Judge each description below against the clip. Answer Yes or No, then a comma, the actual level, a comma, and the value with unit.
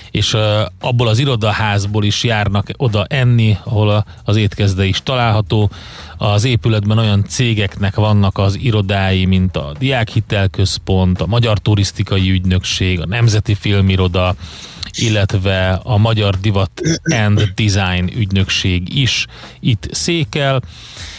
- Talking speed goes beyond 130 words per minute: No, average, 115 wpm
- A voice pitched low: Yes, low, 105 Hz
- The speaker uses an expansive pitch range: No, average, 2.8 semitones